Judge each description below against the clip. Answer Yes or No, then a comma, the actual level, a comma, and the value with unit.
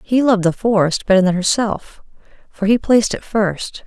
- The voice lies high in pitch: Yes, high, 205 Hz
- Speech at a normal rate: Yes, average, 185 wpm